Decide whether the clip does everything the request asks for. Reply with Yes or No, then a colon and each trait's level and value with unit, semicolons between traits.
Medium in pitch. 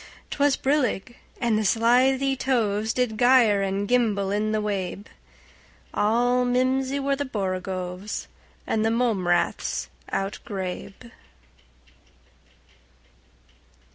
No: high, 225 Hz